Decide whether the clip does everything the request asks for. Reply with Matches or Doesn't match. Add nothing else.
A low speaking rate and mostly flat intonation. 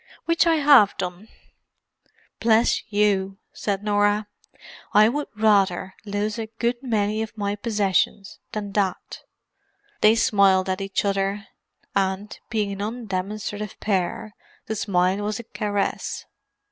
Matches